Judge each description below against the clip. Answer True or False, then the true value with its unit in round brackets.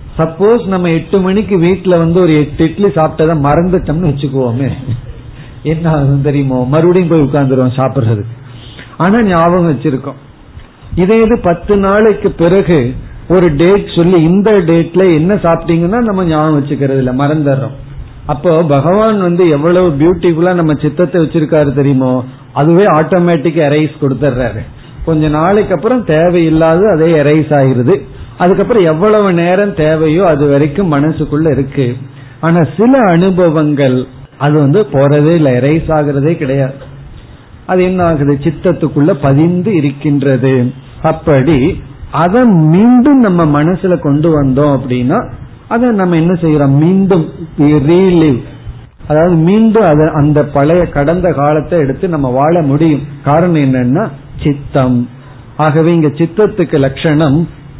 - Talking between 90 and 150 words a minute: True (95 wpm)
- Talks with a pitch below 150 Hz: False (155 Hz)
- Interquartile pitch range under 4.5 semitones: True (3.9 semitones)